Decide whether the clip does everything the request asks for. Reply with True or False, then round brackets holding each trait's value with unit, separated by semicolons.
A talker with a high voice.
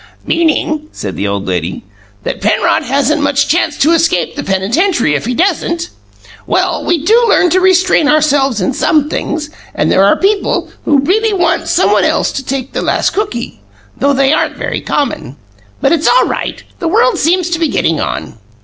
True (300 Hz)